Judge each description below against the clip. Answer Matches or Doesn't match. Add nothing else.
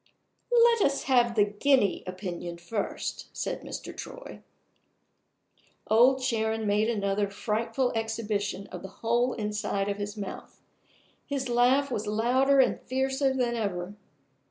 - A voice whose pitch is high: Matches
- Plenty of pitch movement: Doesn't match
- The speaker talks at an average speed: Doesn't match